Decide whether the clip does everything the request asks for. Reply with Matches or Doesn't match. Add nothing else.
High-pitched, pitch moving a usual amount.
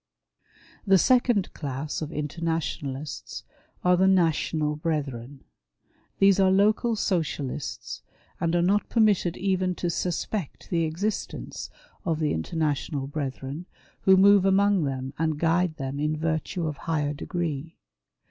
Doesn't match